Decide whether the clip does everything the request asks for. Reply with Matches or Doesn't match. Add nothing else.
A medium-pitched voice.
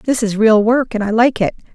Doesn't match